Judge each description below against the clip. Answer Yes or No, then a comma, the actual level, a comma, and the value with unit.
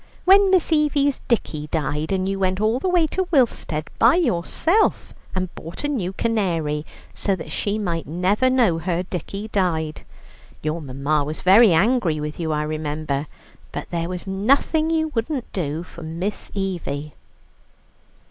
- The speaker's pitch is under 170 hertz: No, medium, 185 Hz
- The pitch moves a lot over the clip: Yes, wide, 7.3 semitones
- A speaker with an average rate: Yes, average, 155 wpm